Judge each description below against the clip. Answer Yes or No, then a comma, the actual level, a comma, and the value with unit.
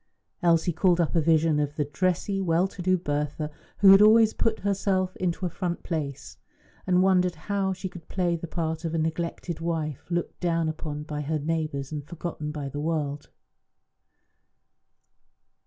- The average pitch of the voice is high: No, medium, 165 Hz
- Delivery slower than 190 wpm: Yes, average, 170 wpm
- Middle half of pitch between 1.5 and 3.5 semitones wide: Yes, average, 3.1 semitones